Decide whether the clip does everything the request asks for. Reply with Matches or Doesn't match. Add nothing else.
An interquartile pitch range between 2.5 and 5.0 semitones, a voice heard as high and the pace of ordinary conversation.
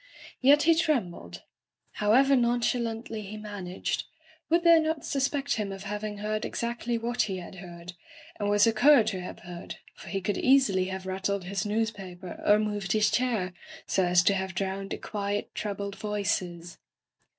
Matches